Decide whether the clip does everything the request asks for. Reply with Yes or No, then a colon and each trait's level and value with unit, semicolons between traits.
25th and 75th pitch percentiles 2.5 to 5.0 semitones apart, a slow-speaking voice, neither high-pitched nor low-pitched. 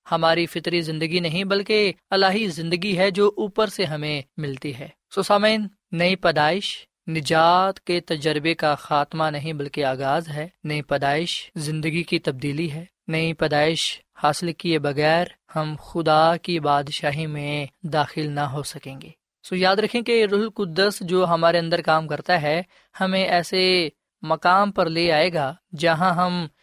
No: average, 3.4 semitones; average, 160 wpm; medium, 165 Hz